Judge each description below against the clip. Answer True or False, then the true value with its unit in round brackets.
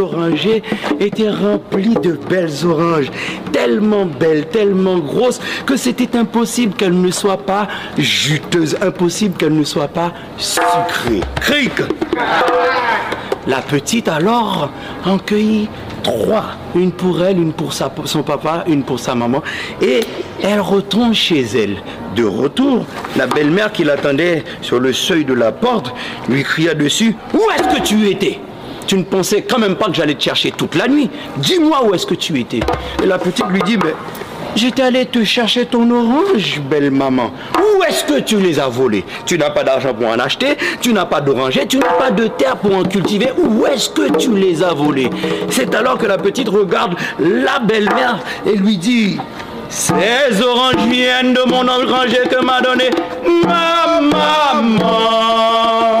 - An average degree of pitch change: False (5.7 semitones)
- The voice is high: True (205 Hz)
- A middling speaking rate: True (165 wpm)